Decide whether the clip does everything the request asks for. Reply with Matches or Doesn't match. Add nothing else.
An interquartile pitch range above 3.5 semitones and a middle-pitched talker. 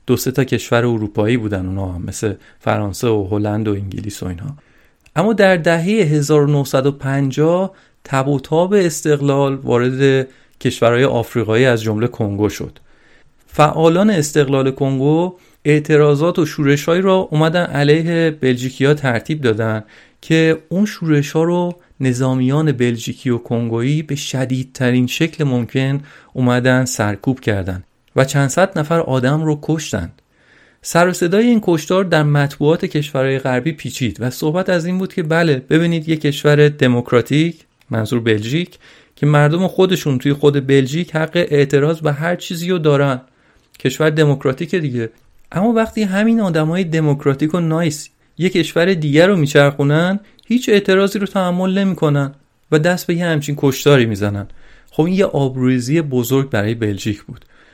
Matches